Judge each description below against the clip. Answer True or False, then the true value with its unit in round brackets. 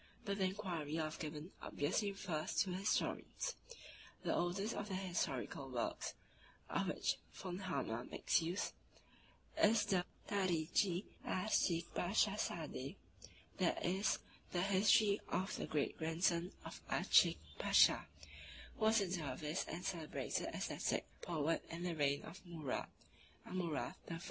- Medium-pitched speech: True (175 Hz)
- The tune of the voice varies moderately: True (3.6 semitones)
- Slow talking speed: True (130 wpm)